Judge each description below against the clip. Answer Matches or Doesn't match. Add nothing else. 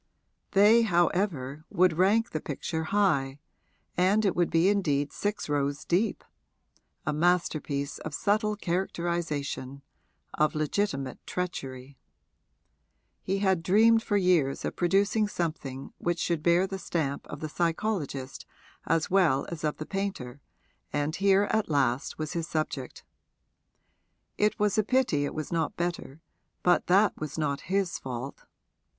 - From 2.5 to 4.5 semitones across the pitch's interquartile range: Doesn't match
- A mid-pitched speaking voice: Matches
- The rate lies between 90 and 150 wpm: Matches